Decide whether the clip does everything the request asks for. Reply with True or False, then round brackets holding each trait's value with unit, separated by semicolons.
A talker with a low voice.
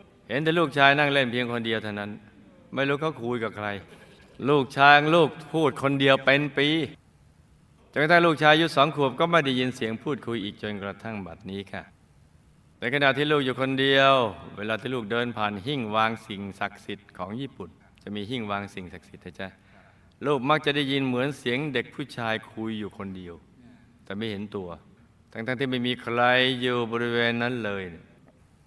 True (120 Hz)